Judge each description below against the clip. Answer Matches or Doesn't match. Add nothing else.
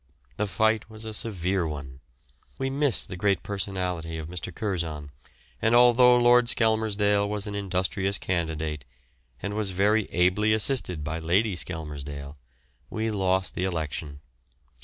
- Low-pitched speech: Matches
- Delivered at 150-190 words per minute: Doesn't match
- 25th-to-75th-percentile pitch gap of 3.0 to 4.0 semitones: Doesn't match